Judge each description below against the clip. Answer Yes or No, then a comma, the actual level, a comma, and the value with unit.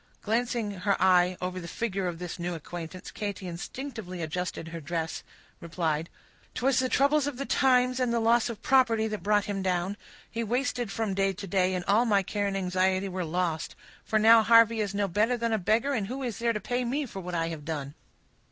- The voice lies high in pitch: Yes, high, 200 Hz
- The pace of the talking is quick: Yes, fast, 215 wpm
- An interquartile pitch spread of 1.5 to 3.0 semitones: No, average, 4.5 semitones